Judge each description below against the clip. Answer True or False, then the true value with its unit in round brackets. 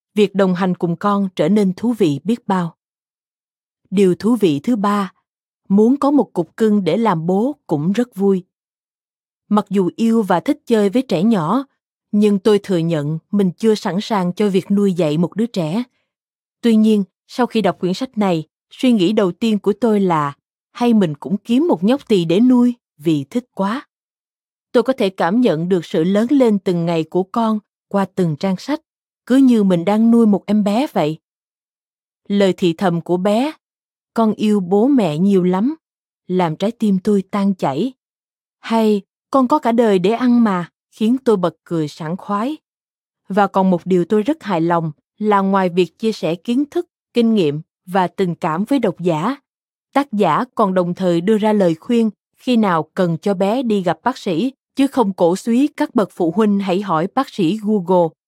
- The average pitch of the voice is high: True (205 Hz)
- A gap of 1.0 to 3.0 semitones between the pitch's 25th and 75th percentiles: False (4.2 semitones)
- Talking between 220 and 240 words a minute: False (195 wpm)